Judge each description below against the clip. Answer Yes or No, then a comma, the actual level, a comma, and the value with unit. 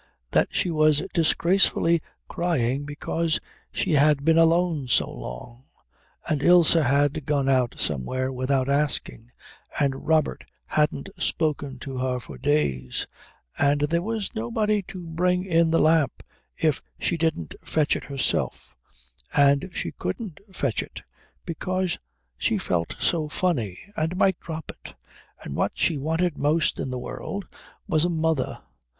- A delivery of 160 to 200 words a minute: No, average, 140 wpm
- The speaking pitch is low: No, medium, 150 Hz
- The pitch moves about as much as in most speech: Yes, average, 3.9 semitones